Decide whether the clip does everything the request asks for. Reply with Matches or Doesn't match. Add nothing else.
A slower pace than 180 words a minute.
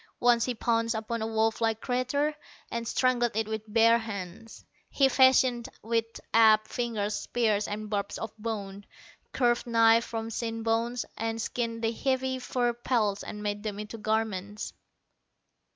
Matches